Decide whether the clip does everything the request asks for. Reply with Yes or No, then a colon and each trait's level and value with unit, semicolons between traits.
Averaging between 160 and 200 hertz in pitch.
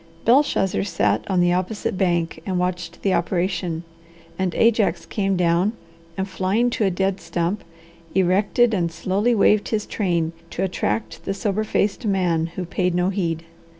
Yes: medium, 185 Hz